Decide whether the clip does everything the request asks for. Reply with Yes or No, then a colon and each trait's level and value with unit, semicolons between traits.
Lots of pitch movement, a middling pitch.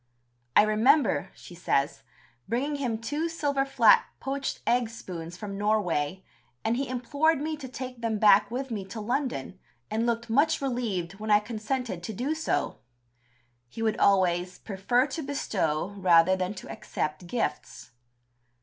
No: wide, 5.8 semitones; high, 220 Hz